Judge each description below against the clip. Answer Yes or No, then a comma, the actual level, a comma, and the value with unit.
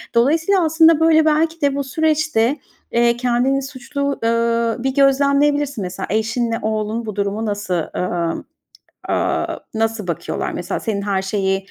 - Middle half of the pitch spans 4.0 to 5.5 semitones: Yes, average, 5.1 semitones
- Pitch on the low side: No, high, 235 Hz